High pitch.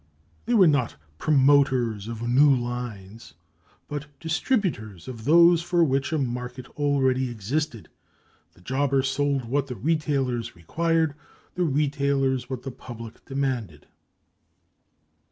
No: low, 135 Hz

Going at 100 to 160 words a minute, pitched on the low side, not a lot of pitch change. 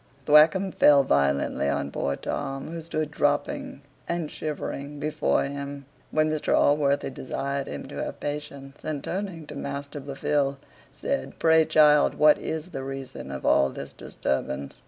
No: average, 150 wpm; medium, 145 Hz; narrow, 2.1 semitones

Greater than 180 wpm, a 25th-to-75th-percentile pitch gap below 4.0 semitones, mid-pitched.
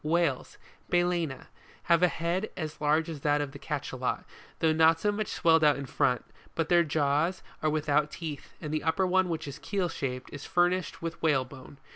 Yes: average, 195 wpm; average, 2.9 semitones; medium, 160 Hz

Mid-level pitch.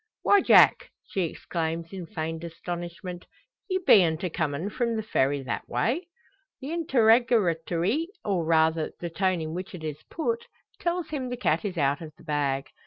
Yes: medium, 175 Hz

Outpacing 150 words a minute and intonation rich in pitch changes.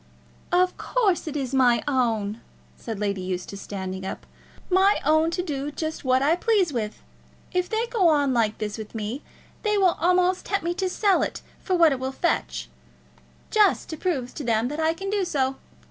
Yes: average, 190 wpm; wide, 7.5 semitones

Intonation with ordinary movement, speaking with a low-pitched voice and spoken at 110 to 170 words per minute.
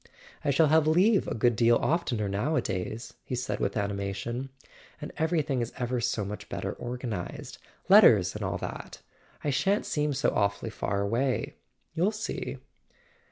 No: wide, 6.1 semitones; low, 125 Hz; average, 150 wpm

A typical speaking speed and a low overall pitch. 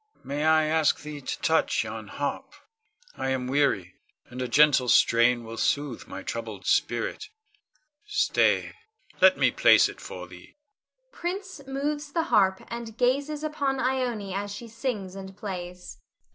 No: average, 145 wpm; high, 190 Hz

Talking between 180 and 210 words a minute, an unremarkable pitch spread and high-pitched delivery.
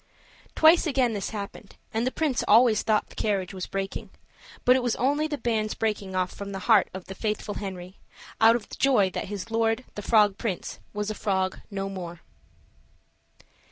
Yes: average, 185 wpm; average, 3.3 semitones; high, 210 Hz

